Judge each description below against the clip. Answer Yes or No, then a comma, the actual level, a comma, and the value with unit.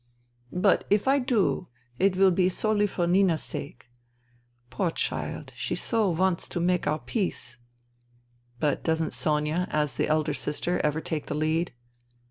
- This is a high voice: No, medium, 165 Hz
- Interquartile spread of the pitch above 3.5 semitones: Yes, average, 4.0 semitones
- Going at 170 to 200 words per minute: No, average, 160 wpm